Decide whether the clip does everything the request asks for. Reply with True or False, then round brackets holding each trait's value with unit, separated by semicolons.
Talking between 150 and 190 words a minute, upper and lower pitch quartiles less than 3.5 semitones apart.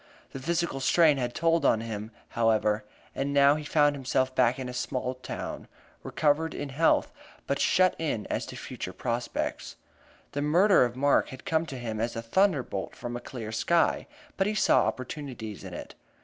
False (180 wpm; 4.5 semitones)